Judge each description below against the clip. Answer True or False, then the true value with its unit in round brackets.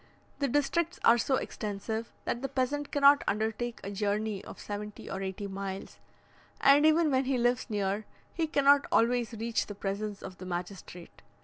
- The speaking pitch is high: True (225 Hz)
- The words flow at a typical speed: True (170 wpm)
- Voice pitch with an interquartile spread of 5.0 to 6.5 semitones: True (5.4 semitones)